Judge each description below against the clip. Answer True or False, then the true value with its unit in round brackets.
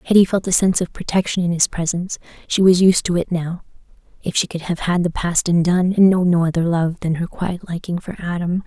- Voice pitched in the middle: True (175 Hz)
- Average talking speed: False (230 wpm)